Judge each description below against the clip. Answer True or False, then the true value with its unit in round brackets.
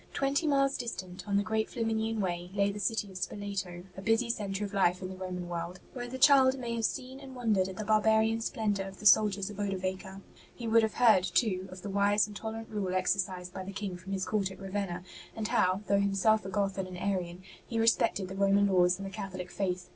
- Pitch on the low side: False (200 Hz)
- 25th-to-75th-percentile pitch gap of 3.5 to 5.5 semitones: False (2.8 semitones)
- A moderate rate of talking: False (230 wpm)